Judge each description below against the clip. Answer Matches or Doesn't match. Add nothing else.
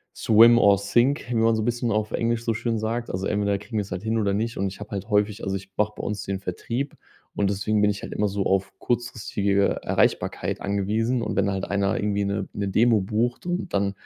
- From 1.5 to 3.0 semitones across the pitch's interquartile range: Matches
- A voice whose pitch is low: Matches